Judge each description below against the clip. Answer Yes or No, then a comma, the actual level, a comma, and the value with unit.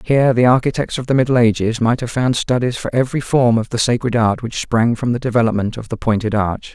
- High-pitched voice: No, low, 120 Hz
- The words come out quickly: Yes, fast, 240 wpm